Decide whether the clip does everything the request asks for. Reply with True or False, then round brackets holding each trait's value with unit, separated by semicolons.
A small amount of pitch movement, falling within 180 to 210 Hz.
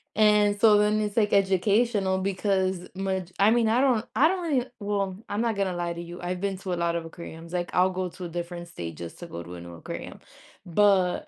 False (3.2 semitones; 190 Hz)